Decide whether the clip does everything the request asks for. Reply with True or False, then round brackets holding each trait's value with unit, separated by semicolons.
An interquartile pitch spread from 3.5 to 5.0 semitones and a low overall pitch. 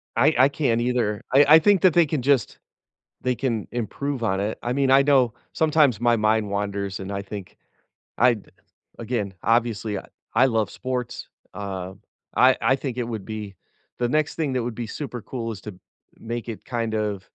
True (3.8 semitones; 120 Hz)